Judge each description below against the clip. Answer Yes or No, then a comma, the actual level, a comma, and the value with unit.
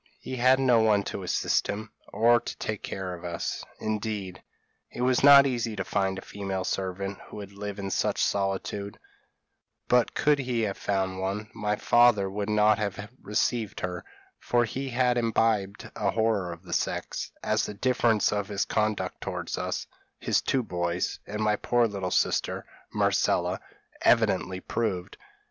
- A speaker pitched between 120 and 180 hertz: No, low, 105 Hz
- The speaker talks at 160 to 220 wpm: Yes, average, 165 wpm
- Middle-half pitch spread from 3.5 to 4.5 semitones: No, average, 3.1 semitones